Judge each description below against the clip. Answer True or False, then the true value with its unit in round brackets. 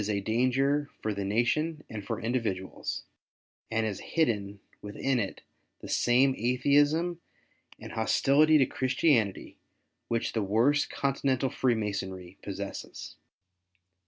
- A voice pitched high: False (120 Hz)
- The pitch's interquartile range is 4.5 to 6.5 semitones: True (5.1 semitones)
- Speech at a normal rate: False (110 wpm)